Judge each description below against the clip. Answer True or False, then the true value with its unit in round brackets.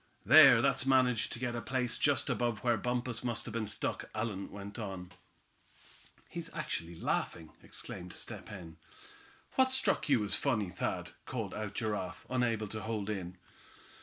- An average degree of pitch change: True (3.9 semitones)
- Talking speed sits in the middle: True (165 wpm)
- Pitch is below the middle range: True (110 Hz)